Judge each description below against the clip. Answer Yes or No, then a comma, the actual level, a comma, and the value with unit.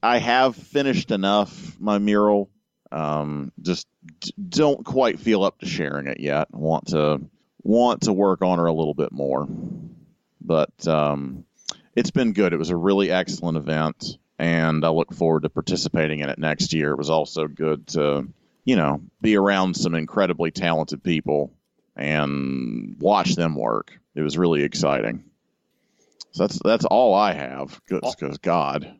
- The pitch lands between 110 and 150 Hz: No, very low, 80 Hz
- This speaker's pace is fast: No, average, 160 wpm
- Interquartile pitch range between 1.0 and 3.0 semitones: No, average, 4.2 semitones